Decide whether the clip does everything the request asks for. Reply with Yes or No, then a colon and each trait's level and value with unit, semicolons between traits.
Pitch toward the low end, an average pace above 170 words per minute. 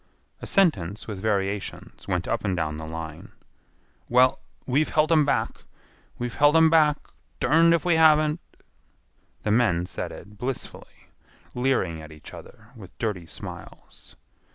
No: low, 115 Hz; average, 145 wpm